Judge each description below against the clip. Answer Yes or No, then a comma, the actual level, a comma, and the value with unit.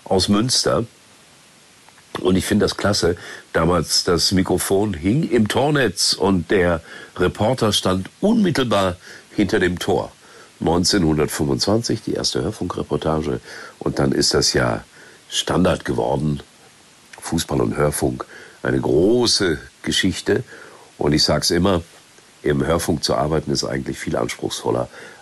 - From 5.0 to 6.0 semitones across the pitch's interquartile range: Yes, average, 5.3 semitones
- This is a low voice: Yes, very low, 90 Hz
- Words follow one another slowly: Yes, slow, 120 wpm